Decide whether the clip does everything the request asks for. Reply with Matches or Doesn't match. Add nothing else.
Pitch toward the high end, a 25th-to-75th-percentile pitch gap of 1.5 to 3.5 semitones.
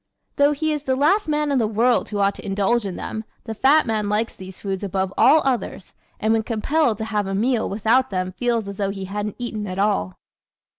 Doesn't match